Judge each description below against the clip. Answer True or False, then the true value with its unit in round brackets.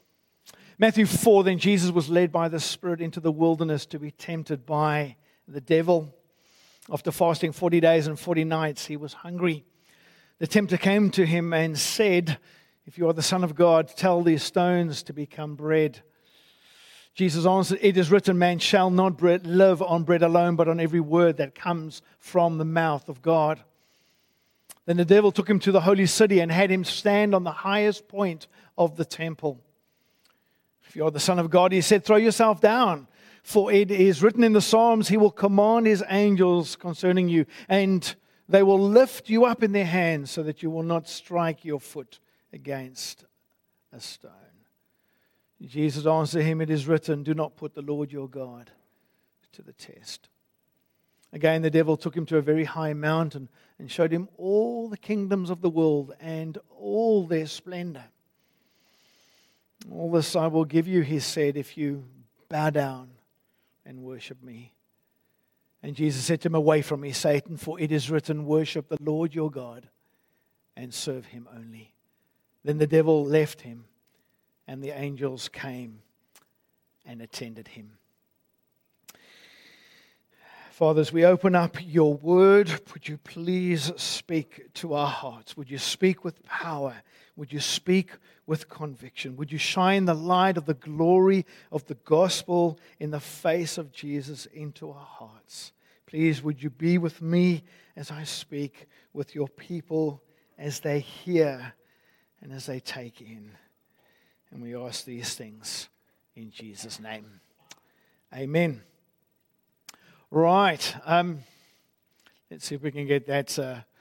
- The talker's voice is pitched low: False (160 Hz)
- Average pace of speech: True (160 wpm)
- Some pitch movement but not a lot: True (3.4 semitones)